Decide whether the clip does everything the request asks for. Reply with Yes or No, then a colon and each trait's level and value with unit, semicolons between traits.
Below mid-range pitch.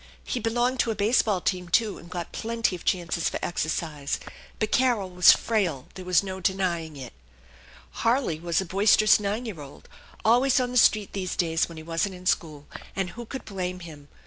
No: medium, 185 Hz